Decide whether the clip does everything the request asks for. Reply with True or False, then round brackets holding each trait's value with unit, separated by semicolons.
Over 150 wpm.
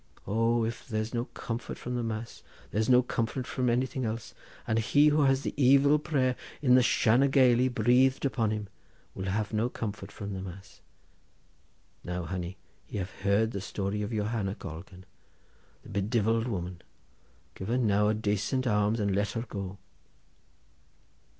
True (165 wpm)